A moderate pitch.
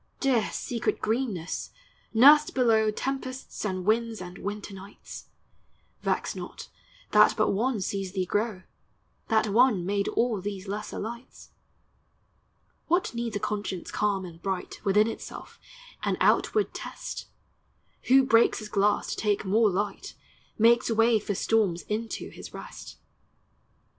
No: high, 215 Hz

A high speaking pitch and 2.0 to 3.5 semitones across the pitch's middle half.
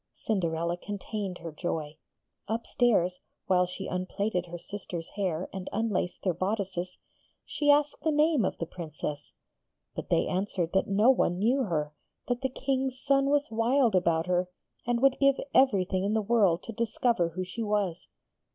No: high, 195 Hz; average, 5.0 semitones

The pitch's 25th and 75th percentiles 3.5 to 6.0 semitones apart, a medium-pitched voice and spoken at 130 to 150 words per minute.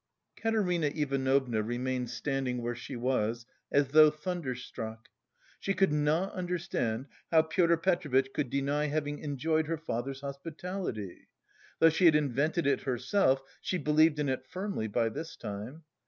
Yes: average, 4.4 semitones; medium, 145 Hz; average, 140 wpm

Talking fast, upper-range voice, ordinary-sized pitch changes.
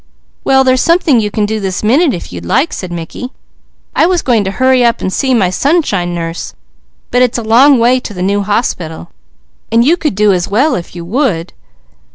No: fast, 210 wpm; high, 225 Hz; wide, 6.0 semitones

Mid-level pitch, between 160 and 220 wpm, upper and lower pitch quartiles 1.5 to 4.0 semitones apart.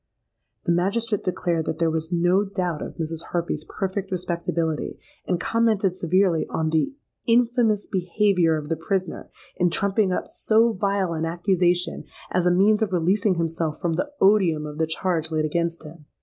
Yes: medium, 180 Hz; average, 165 wpm; average, 3.3 semitones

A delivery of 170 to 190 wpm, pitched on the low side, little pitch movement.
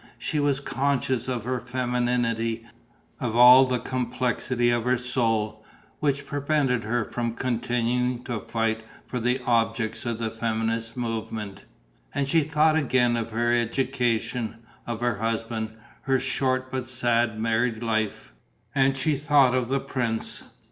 No: average, 140 wpm; low, 120 Hz; narrow, 2.3 semitones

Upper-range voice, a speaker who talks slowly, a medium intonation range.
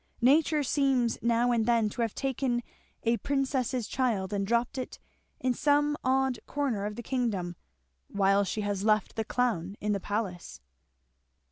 No: high, 235 Hz; average, 155 wpm; average, 4.2 semitones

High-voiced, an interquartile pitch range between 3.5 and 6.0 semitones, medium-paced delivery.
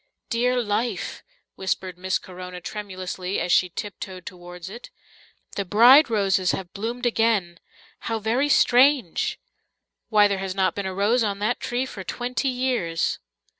Yes: high, 205 Hz; average, 4.5 semitones; average, 145 wpm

